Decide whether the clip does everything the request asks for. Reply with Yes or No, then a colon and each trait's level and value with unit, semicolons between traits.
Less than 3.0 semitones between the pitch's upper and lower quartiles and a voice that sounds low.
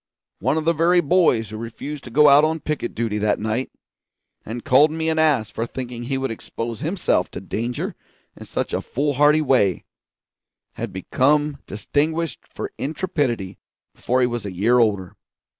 No: average, 5.1 semitones; low, 130 Hz